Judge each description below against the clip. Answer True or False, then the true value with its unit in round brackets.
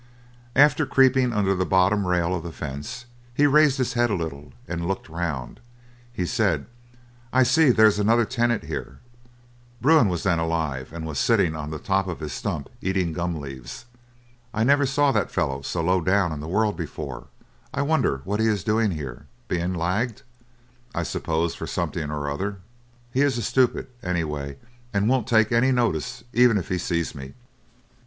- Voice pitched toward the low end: True (95 Hz)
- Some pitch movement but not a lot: False (6.8 semitones)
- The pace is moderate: True (180 wpm)